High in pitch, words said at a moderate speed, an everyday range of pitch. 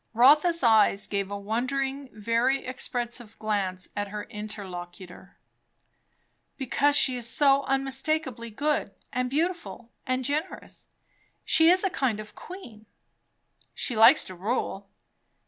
No: high, 245 Hz; slow, 125 wpm; average, 4.7 semitones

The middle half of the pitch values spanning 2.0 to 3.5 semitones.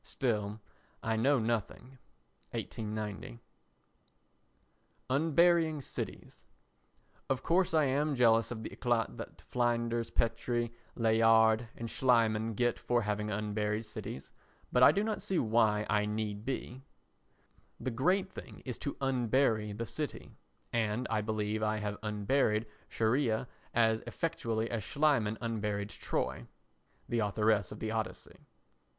Yes: average, 3.0 semitones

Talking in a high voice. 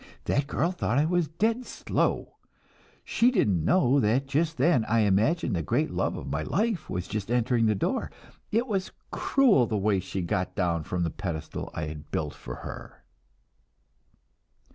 No: low, 115 Hz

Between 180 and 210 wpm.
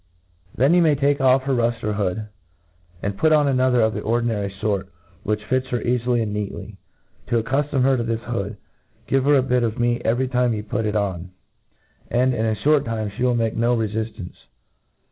Yes: average, 190 wpm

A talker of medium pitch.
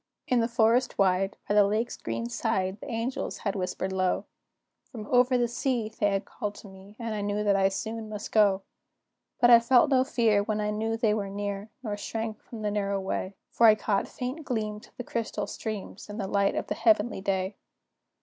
No: high, 210 Hz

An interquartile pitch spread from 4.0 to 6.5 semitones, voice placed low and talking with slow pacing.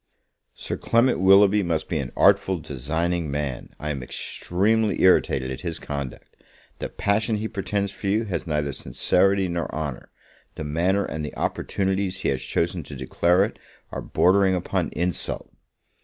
No: average, 4.7 semitones; very low, 90 Hz; average, 155 wpm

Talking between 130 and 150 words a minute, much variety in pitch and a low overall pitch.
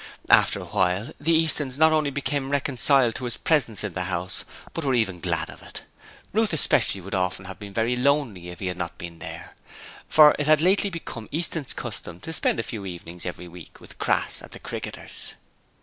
No: fast, 205 wpm; wide, 8.2 semitones; low, 120 Hz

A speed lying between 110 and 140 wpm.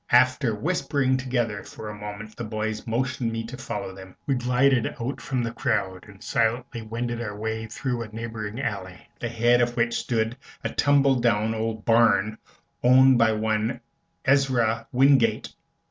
No: average, 165 wpm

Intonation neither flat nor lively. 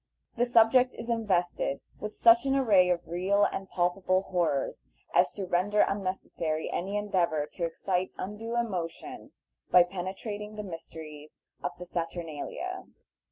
Yes: average, 3.4 semitones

